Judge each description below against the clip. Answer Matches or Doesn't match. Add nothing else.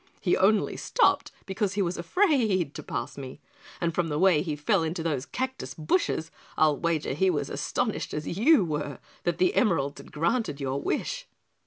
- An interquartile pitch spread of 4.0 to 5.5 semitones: Matches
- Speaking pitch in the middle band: Matches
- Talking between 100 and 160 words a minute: Doesn't match